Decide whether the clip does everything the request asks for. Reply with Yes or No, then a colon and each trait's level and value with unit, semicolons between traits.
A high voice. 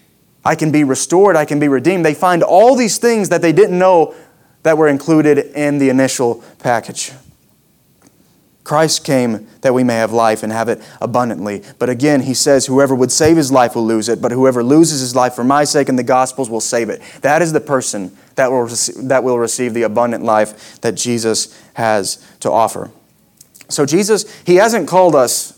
No: low, 135 Hz